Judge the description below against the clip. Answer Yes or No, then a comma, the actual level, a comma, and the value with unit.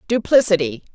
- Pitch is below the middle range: No, high, 190 Hz